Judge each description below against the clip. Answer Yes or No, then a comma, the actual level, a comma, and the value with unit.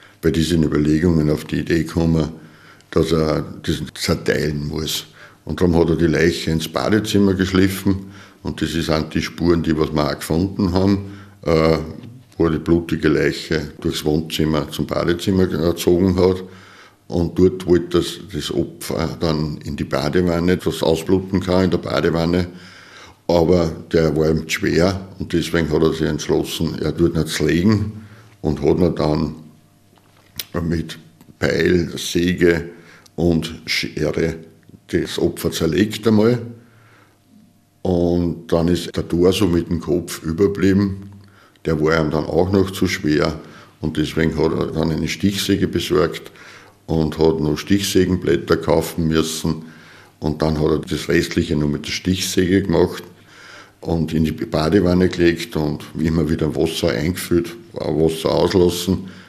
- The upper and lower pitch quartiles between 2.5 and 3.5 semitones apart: Yes, average, 2.9 semitones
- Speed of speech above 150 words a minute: No, average, 145 wpm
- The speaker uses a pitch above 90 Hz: No, very low, 85 Hz